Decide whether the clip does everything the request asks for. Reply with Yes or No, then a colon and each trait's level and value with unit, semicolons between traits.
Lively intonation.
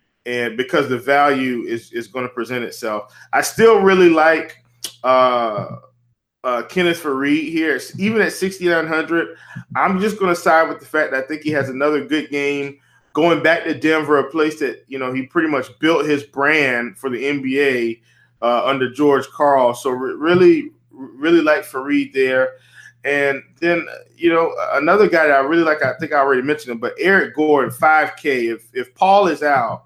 No: average, 4.1 semitones